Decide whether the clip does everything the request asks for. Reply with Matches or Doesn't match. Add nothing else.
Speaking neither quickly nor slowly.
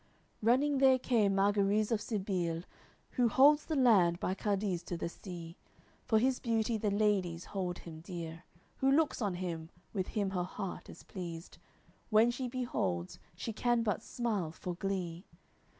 Matches